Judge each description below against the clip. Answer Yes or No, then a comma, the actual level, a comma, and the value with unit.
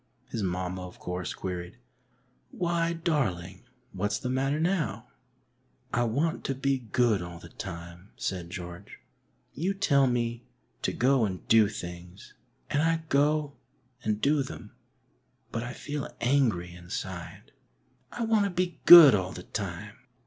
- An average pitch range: No, wide, 8.1 semitones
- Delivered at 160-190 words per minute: No, average, 150 wpm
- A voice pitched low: Yes, low, 115 Hz